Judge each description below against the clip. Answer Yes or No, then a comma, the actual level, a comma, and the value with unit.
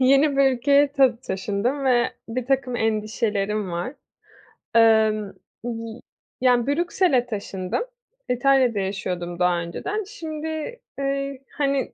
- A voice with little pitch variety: No, average, 4.5 semitones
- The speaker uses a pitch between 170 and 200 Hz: No, high, 245 Hz